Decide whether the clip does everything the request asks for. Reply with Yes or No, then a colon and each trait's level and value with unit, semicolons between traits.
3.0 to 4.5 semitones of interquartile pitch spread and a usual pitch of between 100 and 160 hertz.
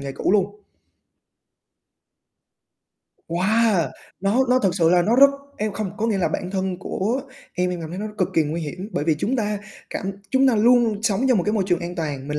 No: average, 4.0 semitones; high, 195 Hz